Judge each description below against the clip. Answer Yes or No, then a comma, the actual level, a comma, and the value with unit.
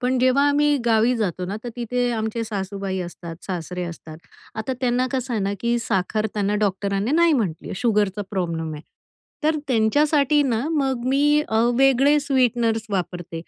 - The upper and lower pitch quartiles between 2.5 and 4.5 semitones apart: No, average, 5.1 semitones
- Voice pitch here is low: No, high, 225 Hz